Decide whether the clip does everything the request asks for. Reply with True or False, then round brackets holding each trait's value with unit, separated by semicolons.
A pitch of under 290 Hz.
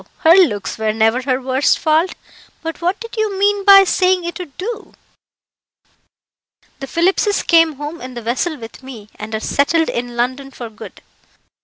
False (305 Hz)